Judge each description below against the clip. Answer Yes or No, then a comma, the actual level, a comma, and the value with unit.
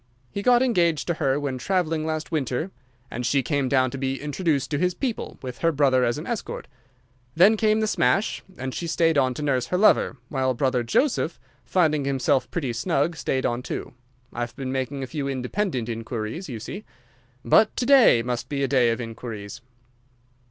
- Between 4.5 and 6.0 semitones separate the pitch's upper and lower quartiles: Yes, average, 5.2 semitones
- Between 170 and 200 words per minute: Yes, average, 185 wpm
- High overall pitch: No, medium, 140 Hz